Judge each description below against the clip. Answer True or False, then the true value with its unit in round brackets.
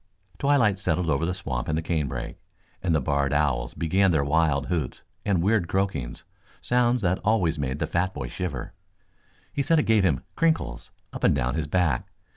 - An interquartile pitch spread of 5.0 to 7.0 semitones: True (5.5 semitones)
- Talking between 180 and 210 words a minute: True (185 wpm)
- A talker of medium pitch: False (85 Hz)